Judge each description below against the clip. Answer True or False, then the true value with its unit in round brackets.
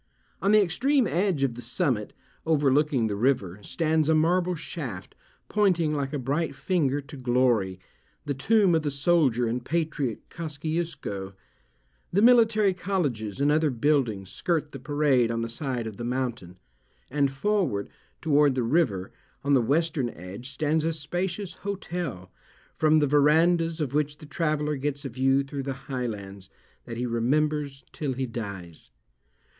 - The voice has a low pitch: False (145 Hz)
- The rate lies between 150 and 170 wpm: True (155 wpm)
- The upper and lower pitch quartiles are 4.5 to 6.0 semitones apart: True (4.9 semitones)